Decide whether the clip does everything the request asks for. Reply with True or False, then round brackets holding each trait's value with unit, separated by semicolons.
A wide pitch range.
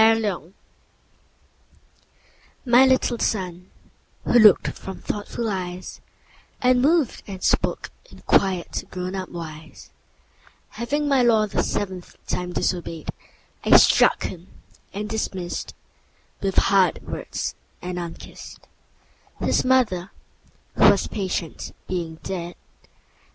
False (4.0 semitones)